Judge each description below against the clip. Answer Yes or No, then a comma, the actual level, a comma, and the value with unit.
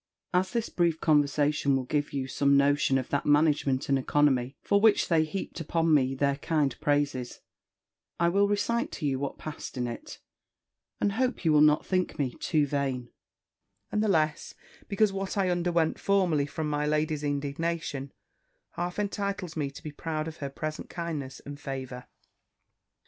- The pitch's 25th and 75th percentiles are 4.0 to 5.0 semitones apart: No, average, 3.6 semitones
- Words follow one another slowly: No, average, 170 wpm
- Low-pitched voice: No, medium, 150 Hz